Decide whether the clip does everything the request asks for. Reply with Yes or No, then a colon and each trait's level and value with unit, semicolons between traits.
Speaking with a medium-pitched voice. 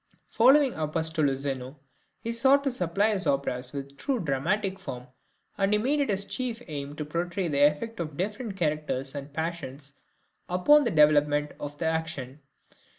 Yes: medium, 160 Hz